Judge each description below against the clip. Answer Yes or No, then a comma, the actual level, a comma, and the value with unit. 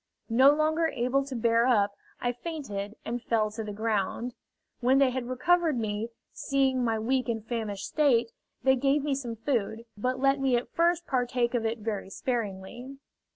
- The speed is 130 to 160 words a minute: No, average, 175 wpm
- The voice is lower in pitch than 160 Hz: No, high, 245 Hz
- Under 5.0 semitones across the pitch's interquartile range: Yes, average, 3.4 semitones